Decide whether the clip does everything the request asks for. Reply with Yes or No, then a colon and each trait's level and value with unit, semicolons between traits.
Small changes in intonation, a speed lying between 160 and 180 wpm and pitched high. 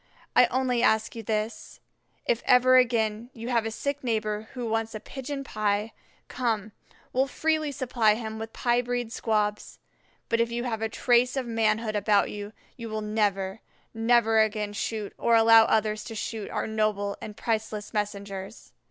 Yes: narrow, 2.0 semitones; average, 170 wpm; high, 225 Hz